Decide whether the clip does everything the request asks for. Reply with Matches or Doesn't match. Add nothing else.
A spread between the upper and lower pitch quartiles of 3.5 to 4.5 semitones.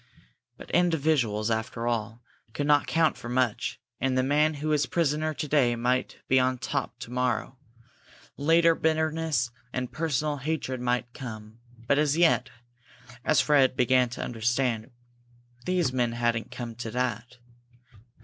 Matches